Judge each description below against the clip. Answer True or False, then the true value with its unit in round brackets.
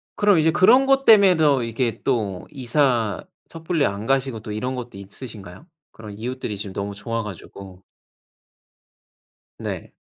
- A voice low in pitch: True (120 Hz)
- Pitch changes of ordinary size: False (6.5 semitones)